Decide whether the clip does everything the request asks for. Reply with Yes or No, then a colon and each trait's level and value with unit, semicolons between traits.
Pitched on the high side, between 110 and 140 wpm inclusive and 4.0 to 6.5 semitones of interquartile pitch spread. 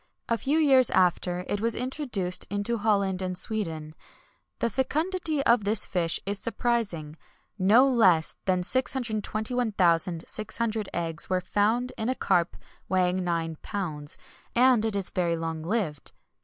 Yes: high, 205 Hz; slow, 135 wpm; average, 4.9 semitones